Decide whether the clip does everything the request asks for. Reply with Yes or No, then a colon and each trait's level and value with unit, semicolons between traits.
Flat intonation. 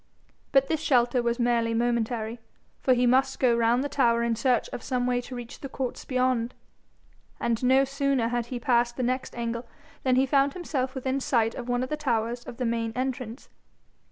Yes: narrow, 2.0 semitones